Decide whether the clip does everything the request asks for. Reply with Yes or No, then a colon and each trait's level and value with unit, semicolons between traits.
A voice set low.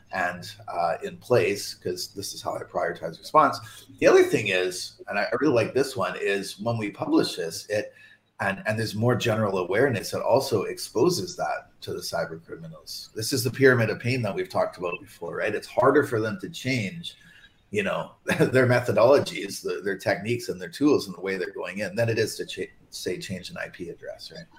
Yes: low, 125 Hz